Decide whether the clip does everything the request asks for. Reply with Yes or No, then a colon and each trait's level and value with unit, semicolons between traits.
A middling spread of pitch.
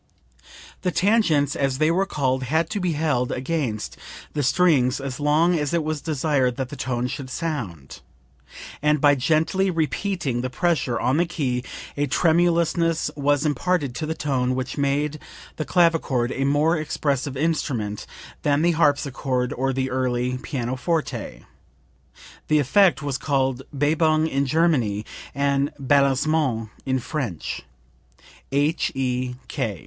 Yes: average, 3.7 semitones